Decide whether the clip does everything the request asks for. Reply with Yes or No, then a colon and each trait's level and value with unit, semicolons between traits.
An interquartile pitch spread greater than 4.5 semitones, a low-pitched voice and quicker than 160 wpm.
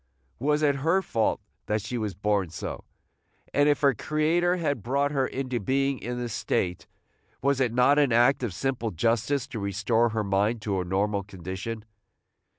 Yes: average, 5.2 semitones; low, 120 Hz; average, 175 wpm